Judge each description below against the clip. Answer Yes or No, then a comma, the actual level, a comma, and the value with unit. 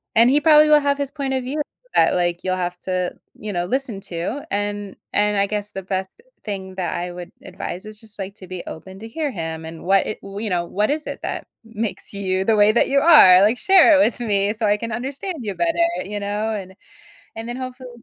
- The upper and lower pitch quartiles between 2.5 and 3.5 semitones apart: No, average, 5.3 semitones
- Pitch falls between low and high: No, high, 210 Hz